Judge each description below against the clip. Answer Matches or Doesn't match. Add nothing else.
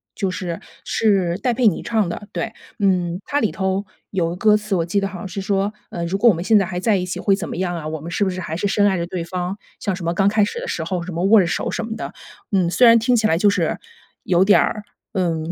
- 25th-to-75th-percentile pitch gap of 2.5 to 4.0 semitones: Matches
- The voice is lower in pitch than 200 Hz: Matches